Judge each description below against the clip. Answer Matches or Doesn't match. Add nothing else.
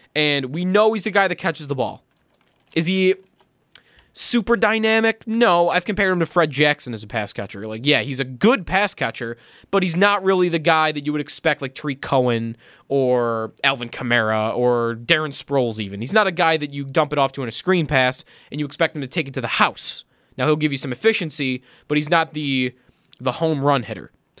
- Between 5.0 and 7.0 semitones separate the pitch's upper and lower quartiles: Matches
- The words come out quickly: Matches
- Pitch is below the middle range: Doesn't match